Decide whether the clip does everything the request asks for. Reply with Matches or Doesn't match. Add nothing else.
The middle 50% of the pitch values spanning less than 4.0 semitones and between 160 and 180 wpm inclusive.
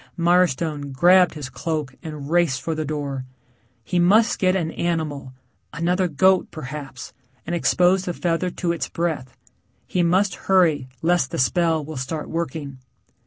Doesn't match